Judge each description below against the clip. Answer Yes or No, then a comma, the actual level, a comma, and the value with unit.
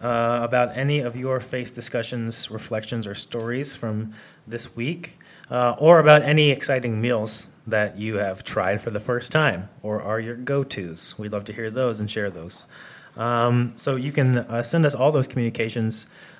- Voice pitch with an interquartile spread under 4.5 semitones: Yes, average, 3.5 semitones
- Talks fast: No, average, 185 wpm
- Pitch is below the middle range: Yes, low, 120 Hz